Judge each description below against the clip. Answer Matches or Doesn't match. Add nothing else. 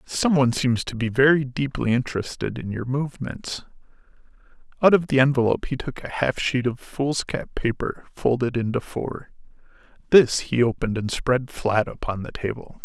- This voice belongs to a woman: Doesn't match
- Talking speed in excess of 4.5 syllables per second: Matches